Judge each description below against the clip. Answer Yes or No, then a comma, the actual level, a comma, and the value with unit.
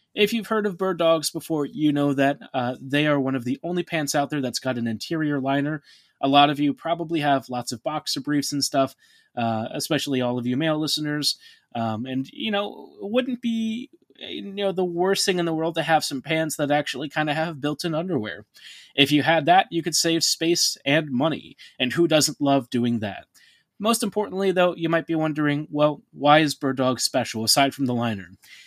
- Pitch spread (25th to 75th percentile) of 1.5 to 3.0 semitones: No, average, 3.6 semitones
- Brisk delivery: Yes, fast, 215 wpm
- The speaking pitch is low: No, medium, 150 Hz